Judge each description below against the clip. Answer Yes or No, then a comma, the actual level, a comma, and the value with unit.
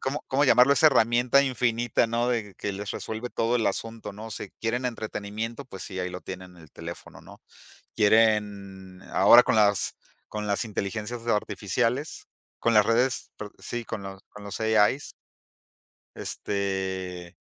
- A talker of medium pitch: No, low, 110 Hz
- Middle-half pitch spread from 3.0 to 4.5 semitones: Yes, average, 3.3 semitones